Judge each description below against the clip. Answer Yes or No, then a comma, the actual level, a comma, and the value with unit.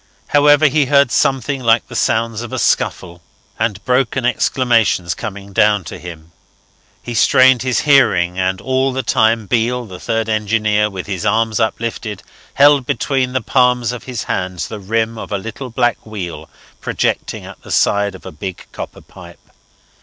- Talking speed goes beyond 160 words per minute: Yes, average, 170 wpm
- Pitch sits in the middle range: No, low, 115 Hz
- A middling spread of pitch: Yes, average, 3.9 semitones